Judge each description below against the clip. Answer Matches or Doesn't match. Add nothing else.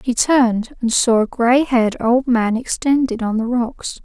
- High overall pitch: Matches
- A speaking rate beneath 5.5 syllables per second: Matches